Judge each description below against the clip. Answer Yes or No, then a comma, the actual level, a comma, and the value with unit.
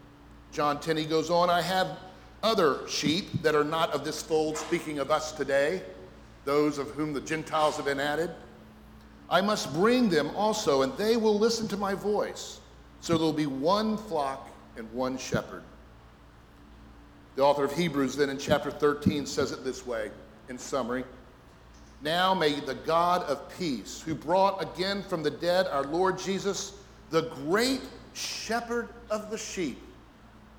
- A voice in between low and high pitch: Yes, medium, 155 Hz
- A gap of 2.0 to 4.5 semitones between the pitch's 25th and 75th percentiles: No, average, 5.3 semitones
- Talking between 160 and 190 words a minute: Yes, average, 165 wpm